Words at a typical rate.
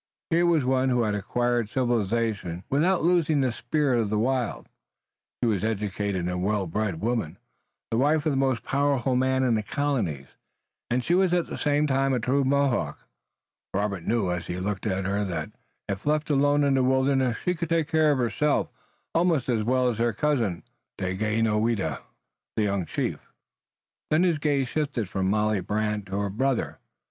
Yes: average, 180 wpm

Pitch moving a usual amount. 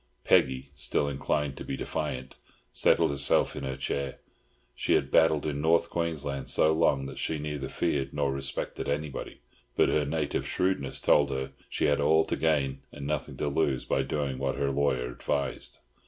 No: narrow, 1.9 semitones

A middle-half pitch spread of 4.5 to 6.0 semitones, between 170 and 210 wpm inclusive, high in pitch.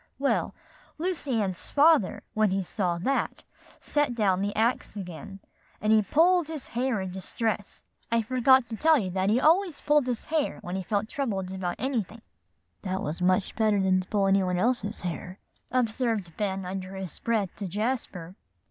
Yes: average, 5.2 semitones; average, 175 wpm; high, 210 Hz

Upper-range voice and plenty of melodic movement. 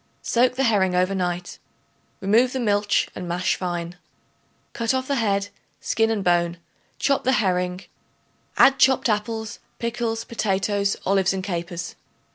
No: high, 200 Hz; average, 4.1 semitones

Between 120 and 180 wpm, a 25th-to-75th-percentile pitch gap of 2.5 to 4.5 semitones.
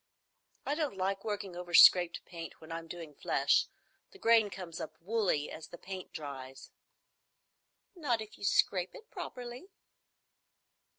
No: slow, 135 wpm; average, 4.9 semitones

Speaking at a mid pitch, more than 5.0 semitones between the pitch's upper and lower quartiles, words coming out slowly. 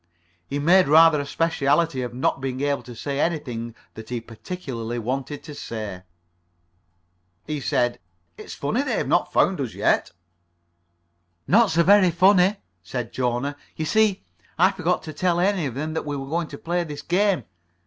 No: medium, 145 Hz; wide, 5.6 semitones; average, 170 wpm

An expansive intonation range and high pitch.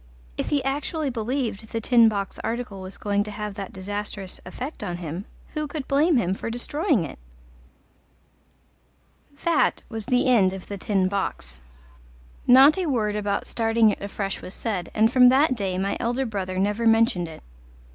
No: average, 4.3 semitones; high, 215 Hz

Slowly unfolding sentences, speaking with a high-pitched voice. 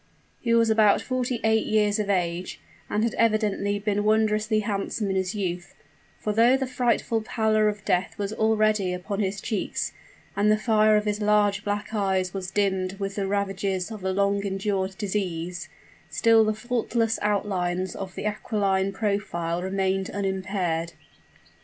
No: average, 160 wpm; high, 205 Hz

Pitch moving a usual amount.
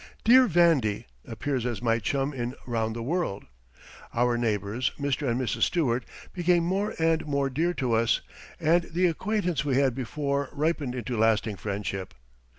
No: wide, 5.9 semitones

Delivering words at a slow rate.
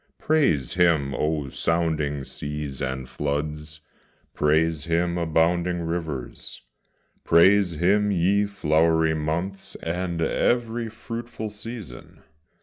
Yes: slow, 95 wpm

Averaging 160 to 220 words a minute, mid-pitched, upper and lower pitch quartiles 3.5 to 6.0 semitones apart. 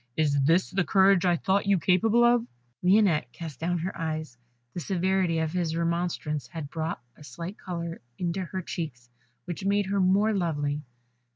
No: average, 170 wpm; medium, 175 Hz; average, 3.1 semitones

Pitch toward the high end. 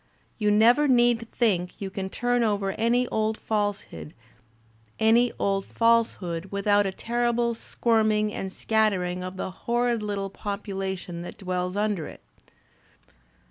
Yes: high, 210 Hz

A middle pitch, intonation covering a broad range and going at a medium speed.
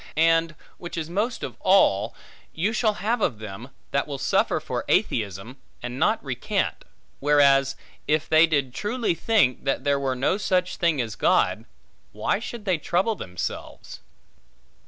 Yes: medium, 155 Hz; wide, 6.5 semitones; average, 155 wpm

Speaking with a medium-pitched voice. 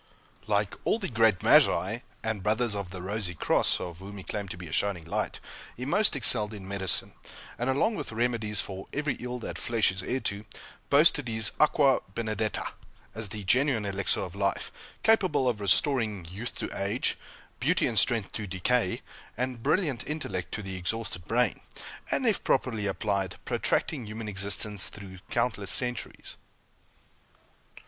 No: low, 105 Hz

